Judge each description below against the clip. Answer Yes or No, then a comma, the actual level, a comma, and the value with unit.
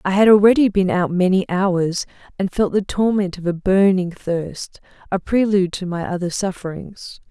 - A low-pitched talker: No, high, 190 Hz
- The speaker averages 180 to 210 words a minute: No, average, 170 wpm